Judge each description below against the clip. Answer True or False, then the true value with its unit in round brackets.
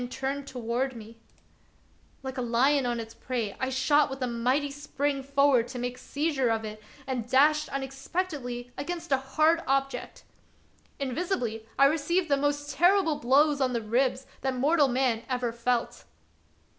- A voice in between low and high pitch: False (265 Hz)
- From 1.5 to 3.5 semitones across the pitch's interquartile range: True (2.9 semitones)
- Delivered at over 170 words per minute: False (160 wpm)